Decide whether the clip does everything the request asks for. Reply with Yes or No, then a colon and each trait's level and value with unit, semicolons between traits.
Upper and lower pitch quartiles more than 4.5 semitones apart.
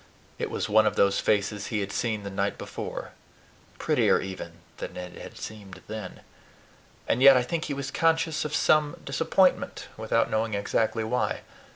Yes: average, 4.9 semitones